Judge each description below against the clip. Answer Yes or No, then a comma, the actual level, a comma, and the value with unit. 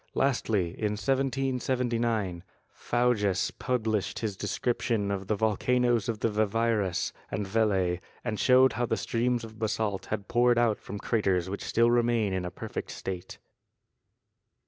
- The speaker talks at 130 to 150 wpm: Yes, average, 140 wpm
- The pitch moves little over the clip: No, average, 3.1 semitones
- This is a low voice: Yes, low, 110 Hz